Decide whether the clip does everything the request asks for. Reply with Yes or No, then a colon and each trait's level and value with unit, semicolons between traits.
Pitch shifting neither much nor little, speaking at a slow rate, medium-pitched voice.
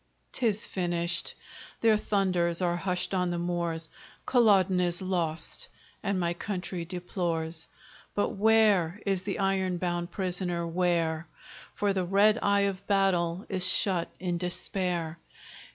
No: narrow, 2.3 semitones; slow, 130 wpm; medium, 180 Hz